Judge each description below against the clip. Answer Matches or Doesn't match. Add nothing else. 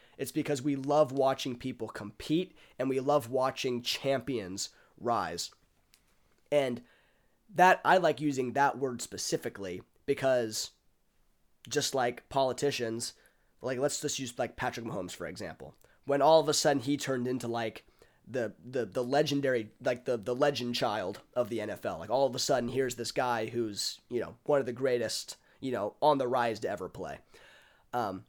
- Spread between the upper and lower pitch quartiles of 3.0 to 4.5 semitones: Matches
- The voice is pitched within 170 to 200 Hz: Doesn't match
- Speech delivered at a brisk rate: Doesn't match